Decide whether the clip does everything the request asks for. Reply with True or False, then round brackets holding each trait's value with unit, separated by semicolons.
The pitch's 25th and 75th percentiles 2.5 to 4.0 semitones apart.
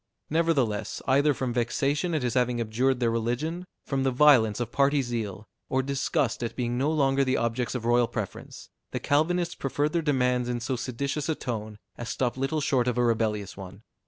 True (3.2 semitones)